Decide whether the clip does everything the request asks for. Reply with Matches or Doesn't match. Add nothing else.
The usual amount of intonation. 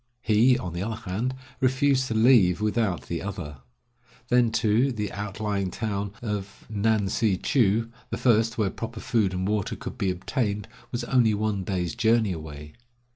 Matches